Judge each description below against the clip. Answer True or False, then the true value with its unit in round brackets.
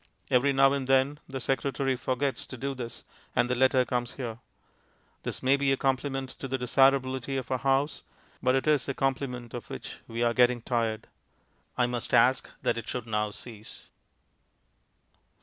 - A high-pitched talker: False (130 Hz)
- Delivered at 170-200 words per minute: True (175 wpm)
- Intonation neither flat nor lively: False (1.8 semitones)